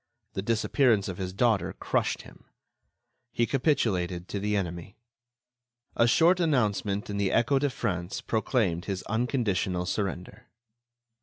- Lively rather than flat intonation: No, average, 4.2 semitones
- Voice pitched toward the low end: Yes, low, 105 Hz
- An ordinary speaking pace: No, slow, 130 wpm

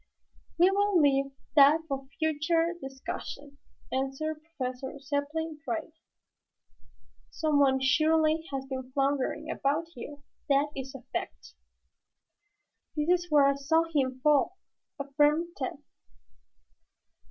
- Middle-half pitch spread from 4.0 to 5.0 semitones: No, average, 2.7 semitones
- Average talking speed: No, slow, 105 wpm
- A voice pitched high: Yes, very high, 290 Hz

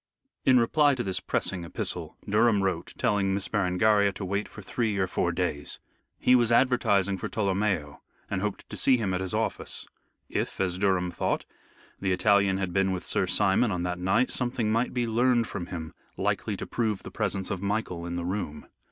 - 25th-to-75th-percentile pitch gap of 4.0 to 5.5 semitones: No, average, 3.3 semitones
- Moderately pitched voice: No, low, 100 Hz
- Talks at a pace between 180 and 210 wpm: Yes, average, 195 wpm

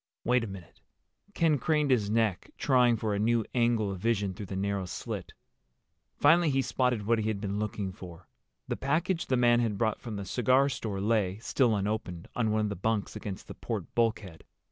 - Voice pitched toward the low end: Yes, low, 110 Hz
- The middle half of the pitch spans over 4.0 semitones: No, average, 3.5 semitones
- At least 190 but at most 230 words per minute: Yes, average, 200 wpm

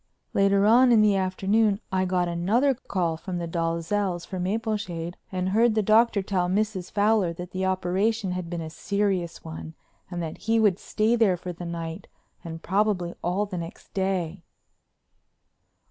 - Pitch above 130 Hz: Yes, high, 190 Hz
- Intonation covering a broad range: No, average, 3.2 semitones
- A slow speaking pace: No, average, 165 wpm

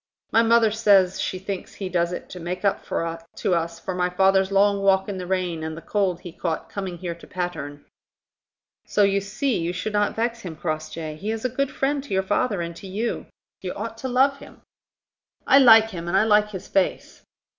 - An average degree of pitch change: Yes, average, 3.5 semitones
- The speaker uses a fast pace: Yes, fast, 215 wpm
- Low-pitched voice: No, high, 190 Hz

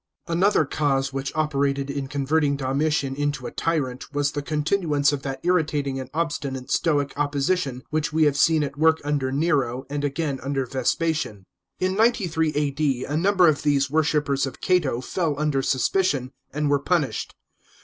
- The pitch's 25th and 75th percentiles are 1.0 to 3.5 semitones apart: Yes, narrow, 2.5 semitones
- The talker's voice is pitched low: No, medium, 145 Hz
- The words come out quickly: No, average, 170 wpm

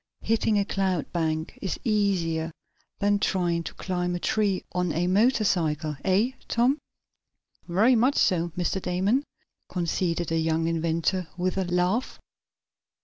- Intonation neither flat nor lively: Yes, average, 3.4 semitones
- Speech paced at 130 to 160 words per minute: Yes, slow, 135 wpm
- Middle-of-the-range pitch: Yes, medium, 180 Hz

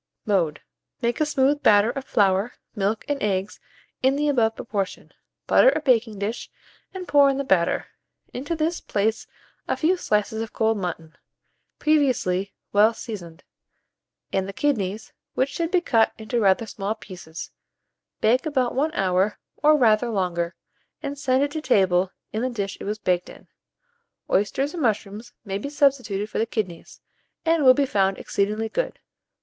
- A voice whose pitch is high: Yes, high, 220 Hz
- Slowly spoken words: No, average, 165 wpm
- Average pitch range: No, wide, 5.9 semitones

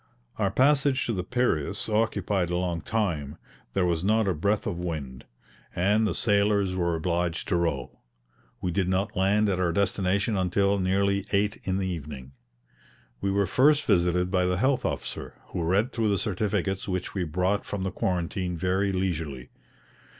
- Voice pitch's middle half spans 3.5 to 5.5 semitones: No, average, 2.7 semitones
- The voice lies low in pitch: Yes, very low, 95 Hz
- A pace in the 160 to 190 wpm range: Yes, average, 170 wpm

